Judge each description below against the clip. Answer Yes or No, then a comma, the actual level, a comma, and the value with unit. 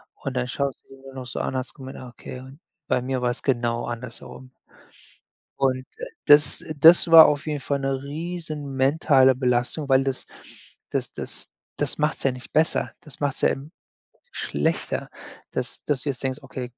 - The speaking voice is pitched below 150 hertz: Yes, low, 135 Hz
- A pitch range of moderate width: No, narrow, 2.3 semitones